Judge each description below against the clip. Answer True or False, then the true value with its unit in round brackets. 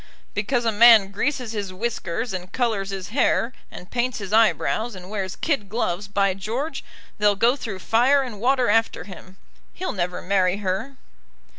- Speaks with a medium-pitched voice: False (210 Hz)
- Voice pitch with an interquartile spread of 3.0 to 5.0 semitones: True (3.8 semitones)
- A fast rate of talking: False (165 wpm)